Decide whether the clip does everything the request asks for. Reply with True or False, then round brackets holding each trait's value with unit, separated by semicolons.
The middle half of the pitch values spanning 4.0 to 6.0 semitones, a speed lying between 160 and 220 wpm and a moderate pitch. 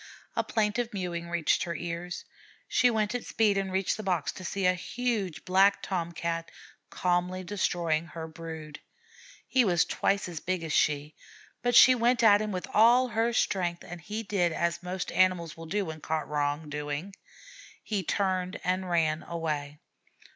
False (3.6 semitones; 170 wpm; 180 Hz)